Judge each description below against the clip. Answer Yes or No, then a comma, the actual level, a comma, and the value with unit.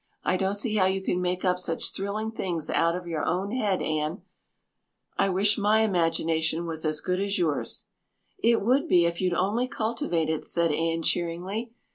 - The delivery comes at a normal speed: Yes, average, 185 wpm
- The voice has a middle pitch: Yes, medium, 180 Hz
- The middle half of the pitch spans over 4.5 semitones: No, average, 3.6 semitones